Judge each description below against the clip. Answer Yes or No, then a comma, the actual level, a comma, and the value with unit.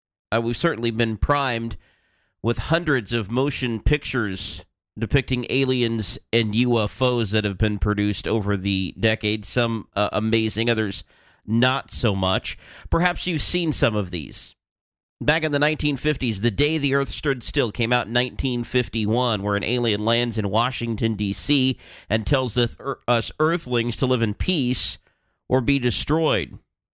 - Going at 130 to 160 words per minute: Yes, average, 145 wpm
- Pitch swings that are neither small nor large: Yes, average, 3.6 semitones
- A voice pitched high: No, low, 120 Hz